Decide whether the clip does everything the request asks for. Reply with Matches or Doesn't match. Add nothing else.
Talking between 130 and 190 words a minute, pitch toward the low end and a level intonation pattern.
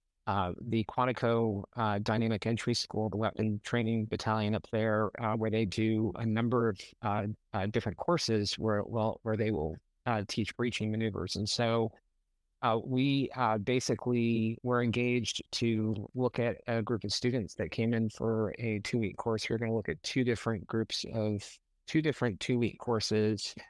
Matches